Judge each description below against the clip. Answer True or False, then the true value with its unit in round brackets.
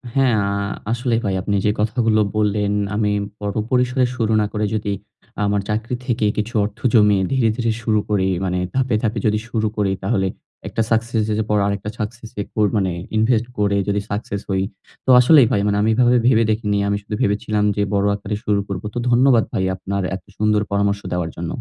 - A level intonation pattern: True (2.1 semitones)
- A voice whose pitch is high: False (105 Hz)